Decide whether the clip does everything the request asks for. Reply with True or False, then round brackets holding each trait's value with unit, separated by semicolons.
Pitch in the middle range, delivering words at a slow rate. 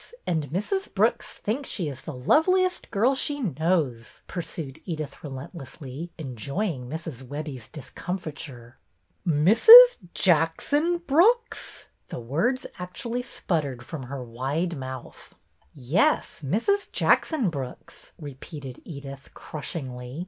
True (155 Hz; 120 wpm)